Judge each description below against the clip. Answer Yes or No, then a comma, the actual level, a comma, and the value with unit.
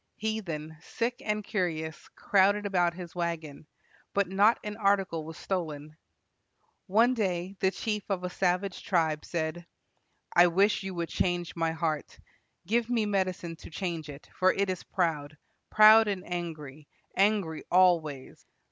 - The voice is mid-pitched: Yes, medium, 180 Hz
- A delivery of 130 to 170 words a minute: Yes, average, 145 wpm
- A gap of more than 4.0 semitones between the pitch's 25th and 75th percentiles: No, average, 3.7 semitones